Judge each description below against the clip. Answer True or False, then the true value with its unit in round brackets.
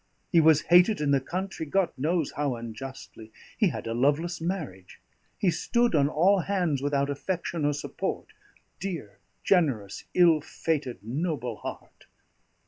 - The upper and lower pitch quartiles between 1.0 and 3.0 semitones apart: False (4.7 semitones)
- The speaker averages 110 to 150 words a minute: True (140 wpm)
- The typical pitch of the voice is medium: True (150 Hz)